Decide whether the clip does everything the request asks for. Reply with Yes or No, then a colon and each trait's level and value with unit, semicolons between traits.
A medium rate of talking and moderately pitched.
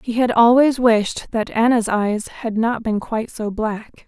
No: average, 190 wpm; high, 225 Hz